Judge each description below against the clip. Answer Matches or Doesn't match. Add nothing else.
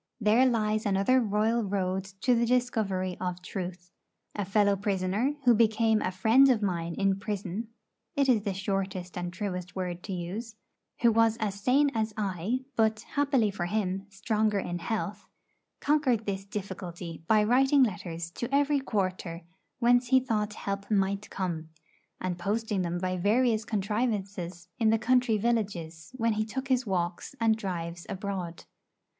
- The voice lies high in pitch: Matches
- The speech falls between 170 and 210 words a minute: Doesn't match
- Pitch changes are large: Doesn't match